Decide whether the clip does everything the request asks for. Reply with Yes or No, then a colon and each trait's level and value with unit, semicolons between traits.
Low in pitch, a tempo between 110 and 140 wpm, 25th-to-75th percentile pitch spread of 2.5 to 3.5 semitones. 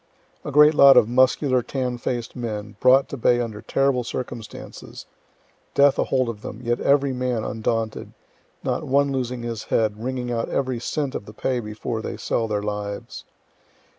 No: low, 120 Hz; average, 165 wpm; average, 2.8 semitones